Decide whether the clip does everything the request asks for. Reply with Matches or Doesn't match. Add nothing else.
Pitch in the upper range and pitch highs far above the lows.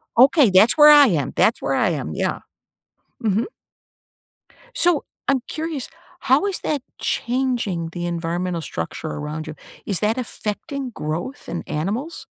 Matches